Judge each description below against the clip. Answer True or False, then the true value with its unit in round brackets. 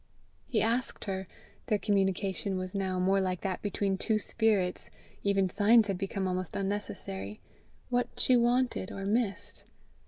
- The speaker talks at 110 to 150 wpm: True (145 wpm)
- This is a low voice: False (195 Hz)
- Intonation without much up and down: True (2.3 semitones)